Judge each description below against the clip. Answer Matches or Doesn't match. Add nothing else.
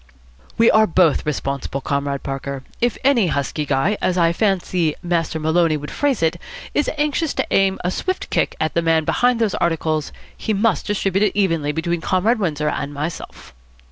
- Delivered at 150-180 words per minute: Matches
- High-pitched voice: Doesn't match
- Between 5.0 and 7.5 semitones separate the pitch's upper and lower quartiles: Matches